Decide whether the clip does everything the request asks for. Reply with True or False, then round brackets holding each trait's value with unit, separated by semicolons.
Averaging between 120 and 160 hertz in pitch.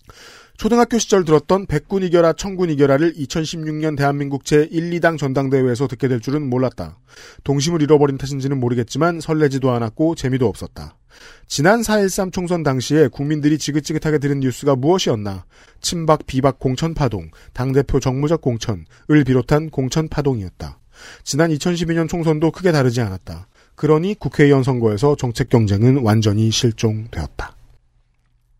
True (140 Hz)